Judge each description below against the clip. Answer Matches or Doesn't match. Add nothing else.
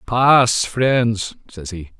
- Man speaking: Matches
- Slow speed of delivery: Matches